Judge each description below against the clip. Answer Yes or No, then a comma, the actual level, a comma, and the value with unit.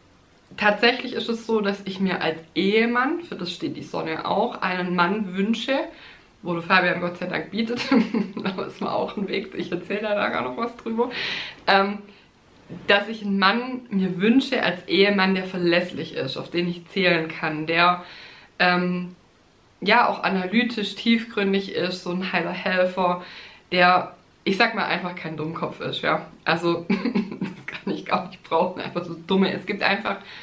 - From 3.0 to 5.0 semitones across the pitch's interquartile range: Yes, average, 3.3 semitones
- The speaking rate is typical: Yes, average, 175 wpm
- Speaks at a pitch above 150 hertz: Yes, high, 190 Hz